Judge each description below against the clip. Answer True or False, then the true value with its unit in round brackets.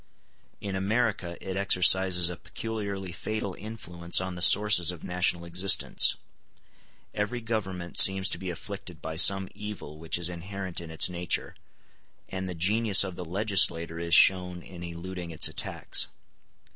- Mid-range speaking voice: False (90 Hz)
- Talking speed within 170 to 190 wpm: False (145 wpm)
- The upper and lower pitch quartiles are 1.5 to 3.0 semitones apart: True (2.4 semitones)